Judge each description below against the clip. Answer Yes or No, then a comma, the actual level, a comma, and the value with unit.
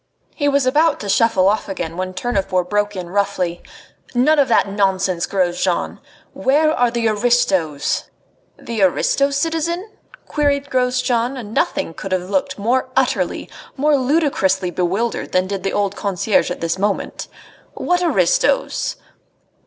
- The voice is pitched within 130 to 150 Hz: No, high, 210 Hz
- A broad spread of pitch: Yes, wide, 6.3 semitones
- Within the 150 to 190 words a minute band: No, average, 140 wpm